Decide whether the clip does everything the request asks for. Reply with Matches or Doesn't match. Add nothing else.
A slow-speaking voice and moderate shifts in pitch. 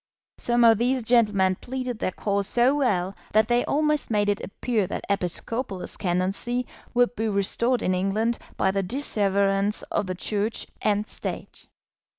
Doesn't match